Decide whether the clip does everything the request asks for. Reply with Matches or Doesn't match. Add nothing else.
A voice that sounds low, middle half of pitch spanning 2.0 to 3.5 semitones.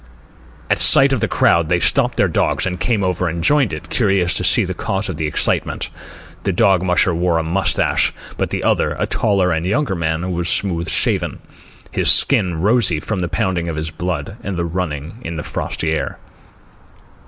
Matches